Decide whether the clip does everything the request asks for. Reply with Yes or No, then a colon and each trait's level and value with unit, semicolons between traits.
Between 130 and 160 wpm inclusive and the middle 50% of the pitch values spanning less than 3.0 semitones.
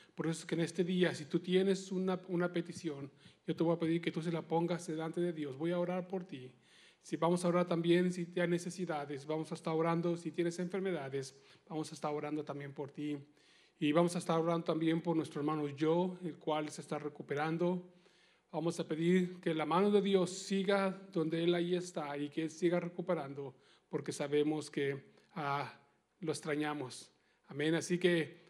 No: average, 200 wpm; narrow, 2.5 semitones